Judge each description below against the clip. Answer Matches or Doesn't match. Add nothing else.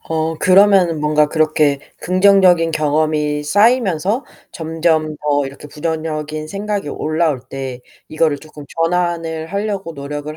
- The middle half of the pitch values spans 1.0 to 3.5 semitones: Matches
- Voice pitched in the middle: Matches